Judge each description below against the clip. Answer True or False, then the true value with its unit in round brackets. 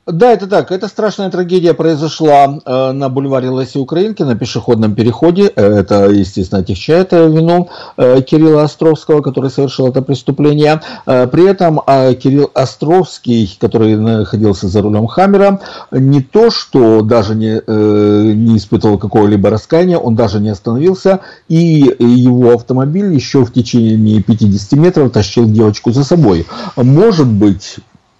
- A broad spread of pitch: True (6.6 semitones)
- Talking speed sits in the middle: True (135 wpm)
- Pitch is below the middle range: True (130 Hz)